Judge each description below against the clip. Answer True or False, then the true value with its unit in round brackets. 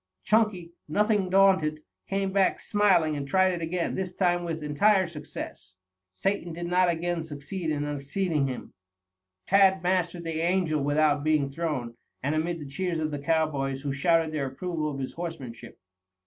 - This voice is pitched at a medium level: True (165 Hz)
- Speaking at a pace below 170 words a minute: True (160 wpm)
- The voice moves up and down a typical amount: True (3.9 semitones)